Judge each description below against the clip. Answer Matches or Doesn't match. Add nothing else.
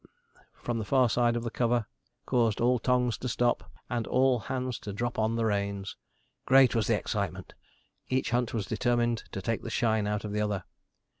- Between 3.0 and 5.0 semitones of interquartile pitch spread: Doesn't match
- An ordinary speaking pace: Matches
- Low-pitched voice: Matches